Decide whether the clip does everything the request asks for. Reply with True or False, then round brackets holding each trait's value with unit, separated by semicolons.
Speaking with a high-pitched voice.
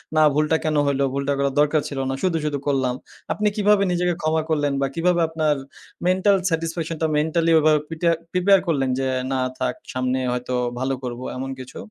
False (155 Hz)